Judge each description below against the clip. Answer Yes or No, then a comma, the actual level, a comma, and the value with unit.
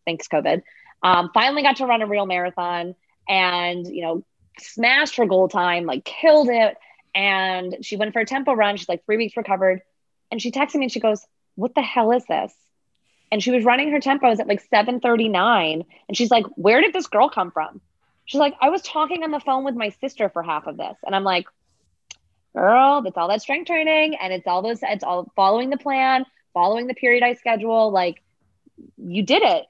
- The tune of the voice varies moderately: No, wide, 6.6 semitones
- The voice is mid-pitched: No, high, 220 Hz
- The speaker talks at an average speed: No, fast, 210 wpm